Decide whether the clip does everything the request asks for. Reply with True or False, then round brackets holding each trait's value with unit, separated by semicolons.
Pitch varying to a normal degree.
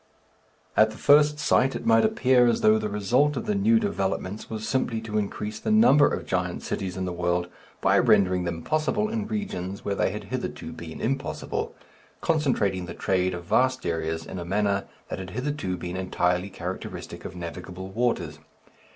False (6.5 semitones)